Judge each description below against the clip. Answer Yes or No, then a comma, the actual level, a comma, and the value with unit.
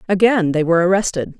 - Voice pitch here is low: No, medium, 180 Hz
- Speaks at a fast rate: No, average, 170 wpm